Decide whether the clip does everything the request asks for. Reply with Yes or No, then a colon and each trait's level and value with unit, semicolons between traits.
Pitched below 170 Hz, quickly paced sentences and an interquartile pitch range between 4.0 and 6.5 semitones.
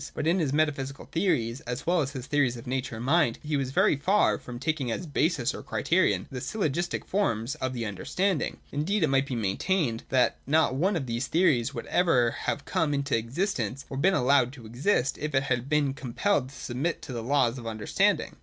Yes: low, 135 Hz; fast, 210 wpm; average, 4.6 semitones